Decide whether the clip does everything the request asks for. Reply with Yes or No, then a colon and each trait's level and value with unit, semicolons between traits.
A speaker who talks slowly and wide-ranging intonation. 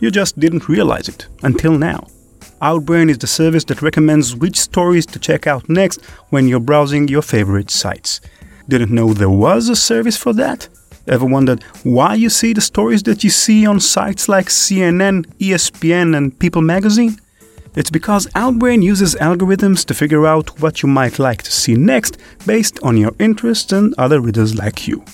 No: average, 180 wpm; wide, 6.9 semitones